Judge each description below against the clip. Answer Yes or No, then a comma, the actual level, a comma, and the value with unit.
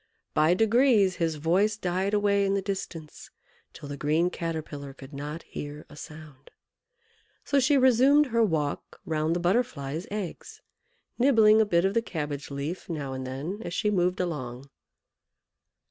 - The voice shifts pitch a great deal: Yes, wide, 5.9 semitones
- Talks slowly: No, average, 155 wpm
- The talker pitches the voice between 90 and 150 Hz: No, medium, 175 Hz